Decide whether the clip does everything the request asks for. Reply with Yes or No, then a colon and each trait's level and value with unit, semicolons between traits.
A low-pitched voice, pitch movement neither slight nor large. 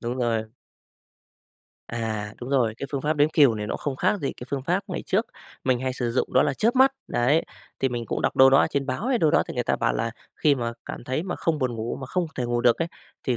Yes: low, 130 Hz; average, 4.2 semitones